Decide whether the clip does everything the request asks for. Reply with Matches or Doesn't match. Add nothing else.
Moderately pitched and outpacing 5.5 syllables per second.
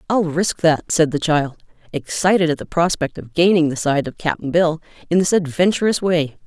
Doesn't match